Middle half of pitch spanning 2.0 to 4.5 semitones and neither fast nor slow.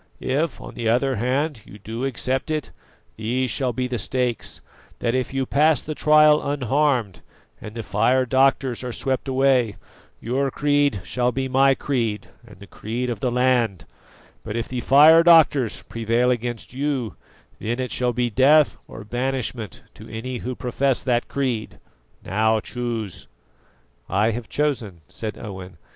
Yes: average, 3.0 semitones; average, 155 wpm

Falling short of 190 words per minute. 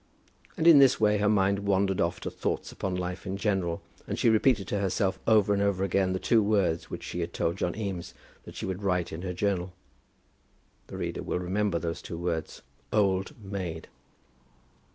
No: average, 195 wpm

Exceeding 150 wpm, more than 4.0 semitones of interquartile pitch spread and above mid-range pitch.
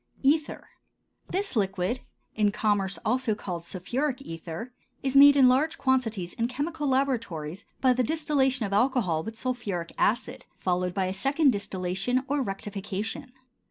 No: average, 140 wpm; wide, 5.6 semitones; high, 235 Hz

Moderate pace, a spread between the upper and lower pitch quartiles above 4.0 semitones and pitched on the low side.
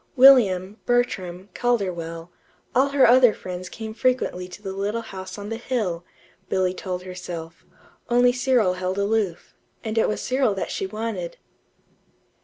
No: average, 145 wpm; average, 4.7 semitones; high, 200 Hz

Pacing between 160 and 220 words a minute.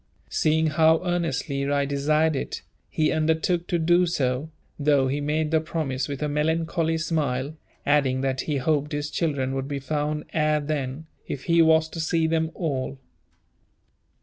Yes: average, 165 wpm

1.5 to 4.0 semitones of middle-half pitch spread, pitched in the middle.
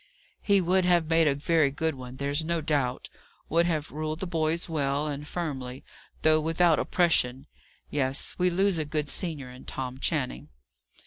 Yes: average, 3.3 semitones; medium, 155 Hz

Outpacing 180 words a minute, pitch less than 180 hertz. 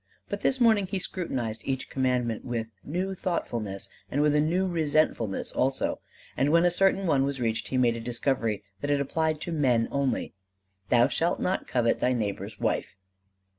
No: average, 175 wpm; low, 135 Hz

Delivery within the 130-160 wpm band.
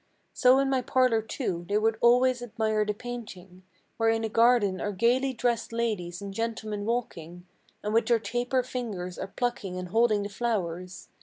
No: average, 175 wpm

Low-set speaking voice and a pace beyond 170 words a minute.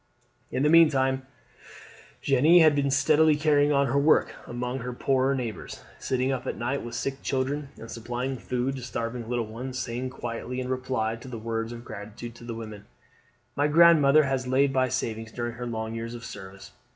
Yes: low, 130 Hz; average, 190 wpm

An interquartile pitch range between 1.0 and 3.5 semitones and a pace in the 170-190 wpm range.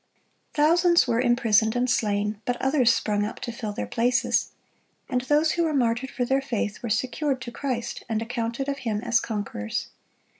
Yes: average, 3.1 semitones; average, 185 wpm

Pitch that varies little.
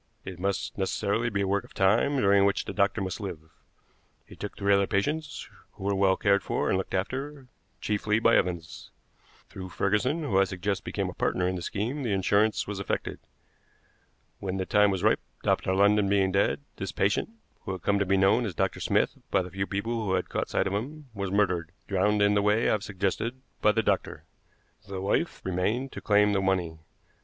Yes: narrow, 1.8 semitones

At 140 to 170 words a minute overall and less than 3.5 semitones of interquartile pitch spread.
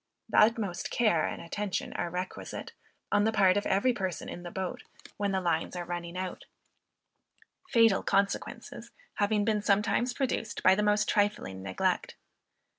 Yes: average, 155 wpm; average, 2.9 semitones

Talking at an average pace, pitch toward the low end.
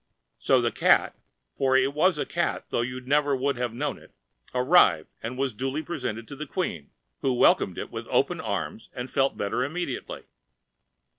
Yes: average, 165 wpm; low, 130 Hz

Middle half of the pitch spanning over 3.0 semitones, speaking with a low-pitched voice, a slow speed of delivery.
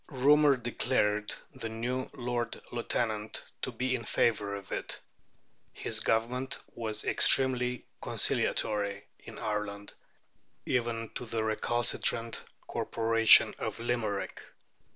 No: narrow, 2.5 semitones; low, 115 Hz; slow, 105 wpm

